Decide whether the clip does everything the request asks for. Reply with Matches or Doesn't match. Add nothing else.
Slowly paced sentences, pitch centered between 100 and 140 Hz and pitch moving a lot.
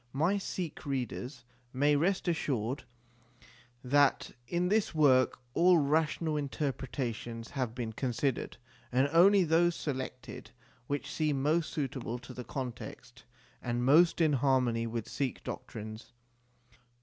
Doesn't match